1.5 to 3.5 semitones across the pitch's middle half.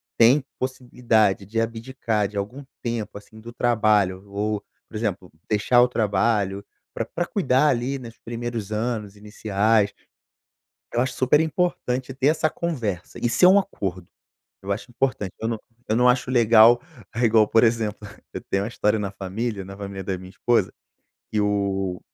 Yes: average, 3.2 semitones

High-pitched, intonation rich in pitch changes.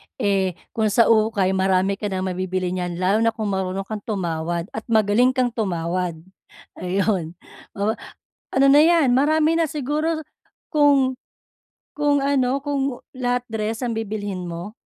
Yes: high, 215 Hz; wide, 5.8 semitones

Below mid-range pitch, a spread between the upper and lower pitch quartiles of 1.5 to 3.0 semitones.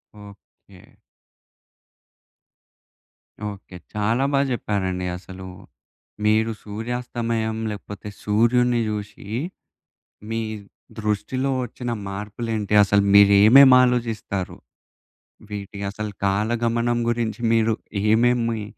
Yes: low, 110 Hz; narrow, 2.5 semitones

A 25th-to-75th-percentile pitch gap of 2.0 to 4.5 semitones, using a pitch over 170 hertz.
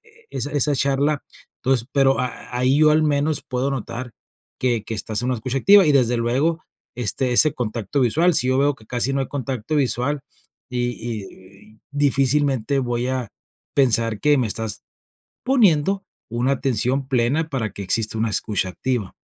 No: average, 3.6 semitones; low, 130 Hz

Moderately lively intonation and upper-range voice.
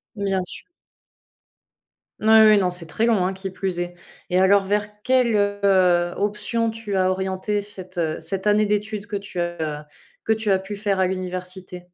No: narrow, 2.3 semitones; high, 195 Hz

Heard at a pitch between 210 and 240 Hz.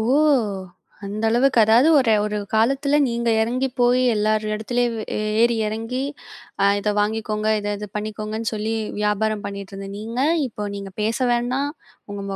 Yes: high, 220 Hz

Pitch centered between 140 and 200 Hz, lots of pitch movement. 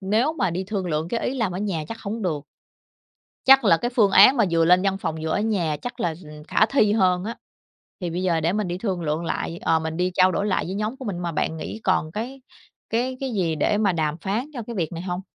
No: high, 190 Hz; average, 4.8 semitones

